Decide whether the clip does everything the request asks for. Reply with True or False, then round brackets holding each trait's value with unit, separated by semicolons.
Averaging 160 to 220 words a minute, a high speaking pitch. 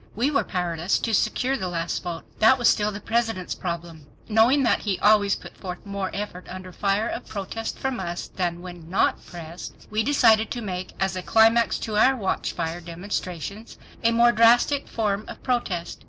True (185 wpm; 200 Hz)